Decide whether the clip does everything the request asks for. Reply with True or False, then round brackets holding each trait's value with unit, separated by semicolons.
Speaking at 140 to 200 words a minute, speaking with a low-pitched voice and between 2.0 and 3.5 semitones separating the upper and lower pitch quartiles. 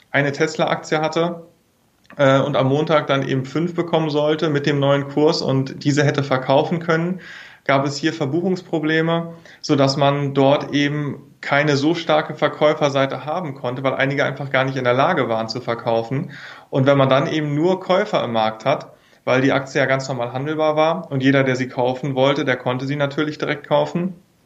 False (190 wpm; 145 Hz; 2.7 semitones)